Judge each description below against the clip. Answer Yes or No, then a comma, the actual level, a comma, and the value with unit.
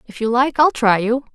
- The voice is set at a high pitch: Yes, high, 240 Hz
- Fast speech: Yes, fast, 270 wpm